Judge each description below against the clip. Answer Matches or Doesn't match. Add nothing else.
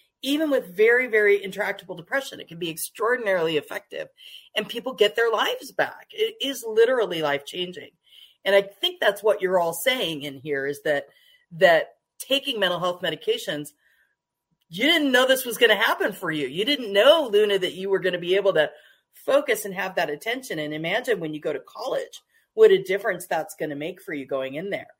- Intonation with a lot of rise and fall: Matches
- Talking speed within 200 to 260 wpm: Matches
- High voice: Matches